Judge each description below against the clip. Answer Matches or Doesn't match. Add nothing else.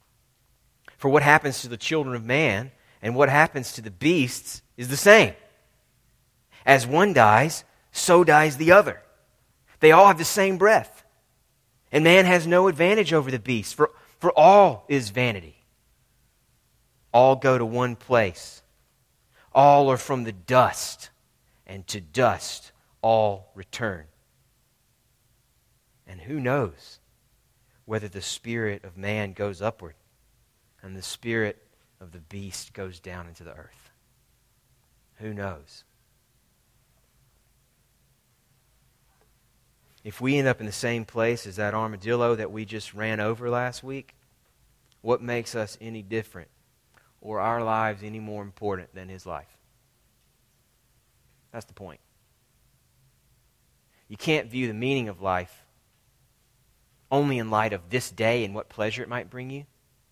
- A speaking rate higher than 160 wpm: Doesn't match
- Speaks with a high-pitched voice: Doesn't match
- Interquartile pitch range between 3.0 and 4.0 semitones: Matches